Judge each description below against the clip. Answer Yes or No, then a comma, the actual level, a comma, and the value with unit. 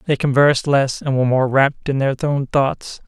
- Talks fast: Yes, fast, 215 wpm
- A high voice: No, low, 135 Hz